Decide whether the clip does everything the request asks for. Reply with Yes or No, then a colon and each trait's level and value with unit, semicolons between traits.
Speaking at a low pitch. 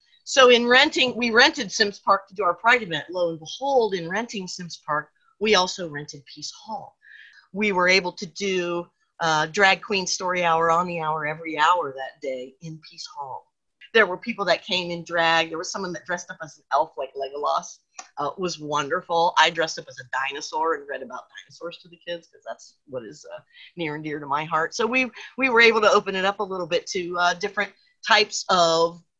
No: medium, 180 Hz